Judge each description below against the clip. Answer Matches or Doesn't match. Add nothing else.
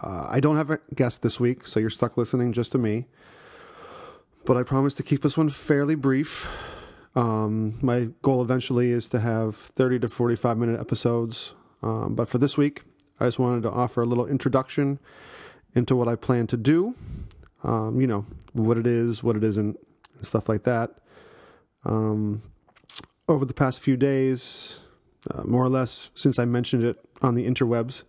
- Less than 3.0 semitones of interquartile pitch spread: Matches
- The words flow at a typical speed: Matches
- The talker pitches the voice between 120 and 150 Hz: Matches